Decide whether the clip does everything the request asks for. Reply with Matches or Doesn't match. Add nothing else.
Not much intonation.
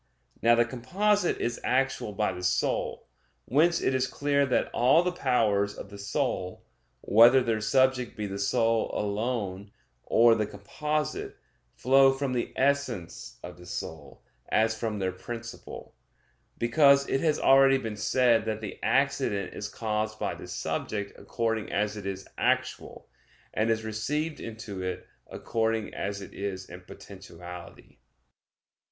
Doesn't match